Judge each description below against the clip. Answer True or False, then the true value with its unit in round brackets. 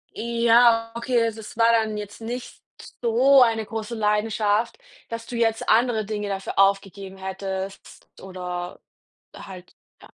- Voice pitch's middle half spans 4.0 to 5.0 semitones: False (2.8 semitones)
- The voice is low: False (220 Hz)